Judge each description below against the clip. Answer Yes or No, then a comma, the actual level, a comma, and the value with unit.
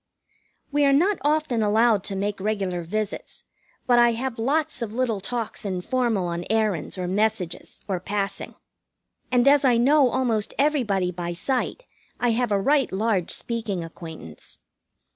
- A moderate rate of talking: Yes, average, 150 wpm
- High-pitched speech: Yes, high, 220 Hz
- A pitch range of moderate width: Yes, average, 4.7 semitones